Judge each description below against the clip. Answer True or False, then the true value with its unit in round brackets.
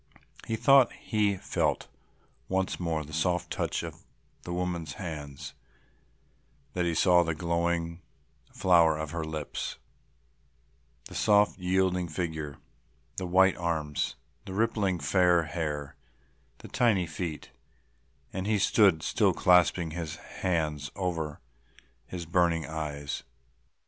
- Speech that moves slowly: True (120 wpm)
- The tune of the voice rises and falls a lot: False (2.9 semitones)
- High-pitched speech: False (85 Hz)